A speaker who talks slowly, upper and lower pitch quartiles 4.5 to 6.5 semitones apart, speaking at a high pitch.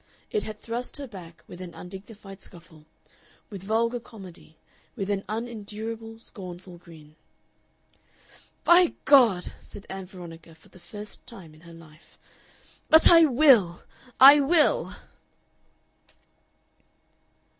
Yes: slow, 115 wpm; average, 5.2 semitones; high, 200 Hz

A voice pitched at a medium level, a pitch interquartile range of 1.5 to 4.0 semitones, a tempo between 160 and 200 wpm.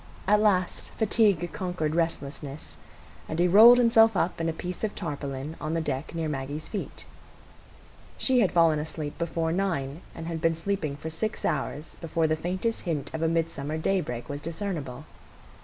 Yes: medium, 165 Hz; average, 3.5 semitones; average, 170 wpm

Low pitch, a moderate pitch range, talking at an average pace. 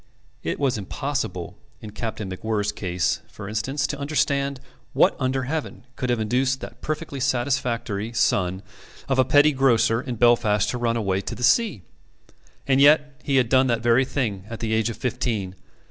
Yes: low, 120 Hz; average, 3.9 semitones; average, 170 wpm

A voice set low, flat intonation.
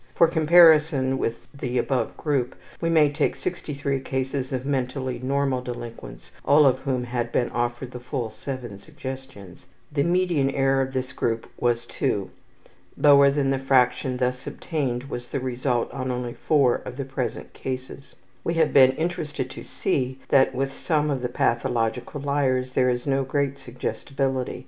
Yes: low, 130 Hz; narrow, 2.1 semitones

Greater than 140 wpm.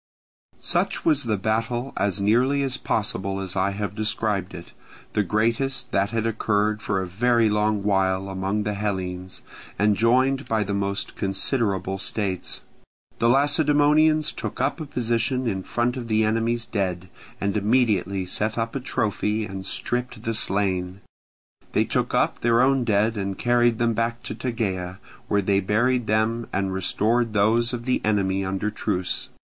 Yes: average, 160 wpm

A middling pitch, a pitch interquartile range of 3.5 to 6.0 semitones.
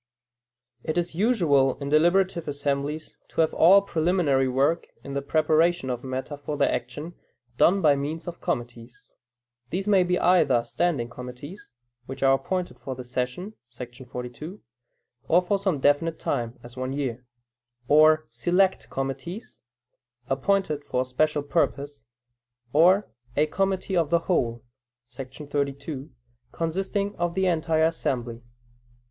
Yes: medium, 150 Hz; average, 4.7 semitones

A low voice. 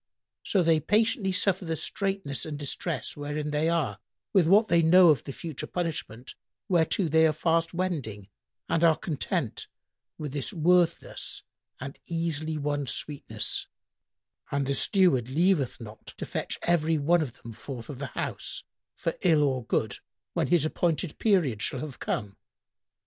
No: medium, 155 Hz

